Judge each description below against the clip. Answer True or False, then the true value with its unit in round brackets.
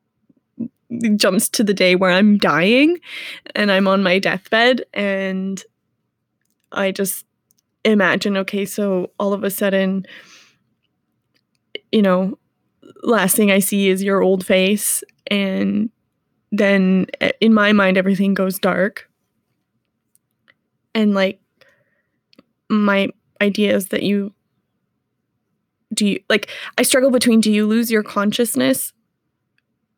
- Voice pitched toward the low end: False (200 Hz)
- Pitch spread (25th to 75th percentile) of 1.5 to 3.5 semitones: True (2.6 semitones)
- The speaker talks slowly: True (120 wpm)